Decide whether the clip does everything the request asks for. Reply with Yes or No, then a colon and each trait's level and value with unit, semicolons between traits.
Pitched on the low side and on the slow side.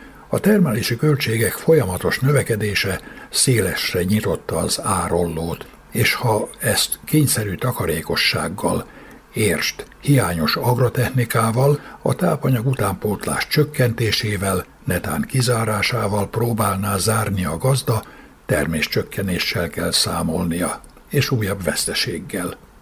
Yes: low, 115 Hz; slow, 90 wpm